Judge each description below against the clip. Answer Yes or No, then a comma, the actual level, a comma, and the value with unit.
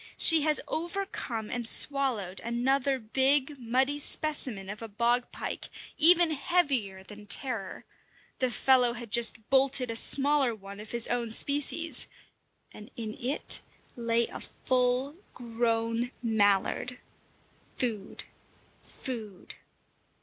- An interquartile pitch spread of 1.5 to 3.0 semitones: No, average, 3.5 semitones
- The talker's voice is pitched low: No, high, 245 Hz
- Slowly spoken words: Yes, slow, 115 wpm